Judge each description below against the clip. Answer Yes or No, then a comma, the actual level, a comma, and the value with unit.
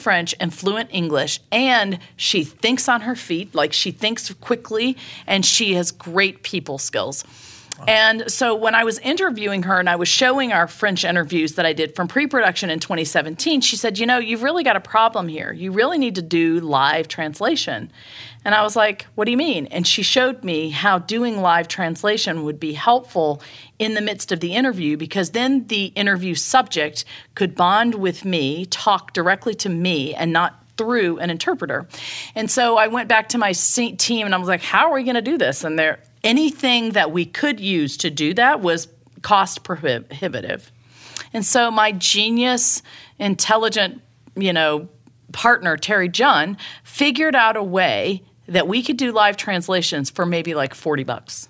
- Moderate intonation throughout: No, wide, 5.7 semitones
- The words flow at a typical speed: Yes, average, 185 wpm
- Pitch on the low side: No, high, 190 Hz